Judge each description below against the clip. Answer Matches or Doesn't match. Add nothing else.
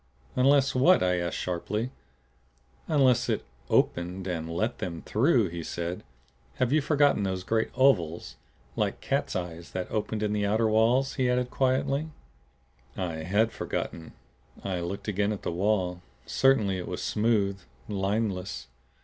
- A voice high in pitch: Doesn't match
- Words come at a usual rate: Matches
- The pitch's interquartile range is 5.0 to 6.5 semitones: Matches